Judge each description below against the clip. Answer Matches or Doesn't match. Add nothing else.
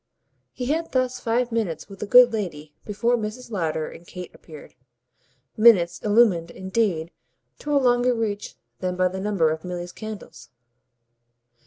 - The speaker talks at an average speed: Matches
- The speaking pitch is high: Matches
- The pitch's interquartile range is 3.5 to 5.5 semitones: Matches